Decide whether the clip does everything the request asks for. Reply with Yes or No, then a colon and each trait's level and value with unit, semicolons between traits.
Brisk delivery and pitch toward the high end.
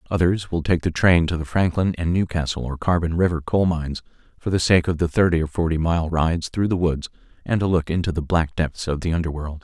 No: fast, 235 wpm; very low, 85 Hz